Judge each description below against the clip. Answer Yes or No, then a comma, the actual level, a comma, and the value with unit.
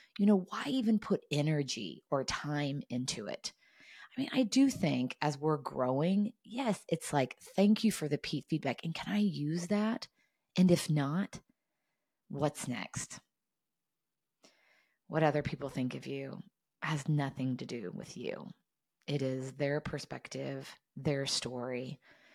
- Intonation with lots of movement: Yes, wide, 6.7 semitones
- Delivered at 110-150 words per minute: Yes, average, 145 wpm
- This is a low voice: No, medium, 155 Hz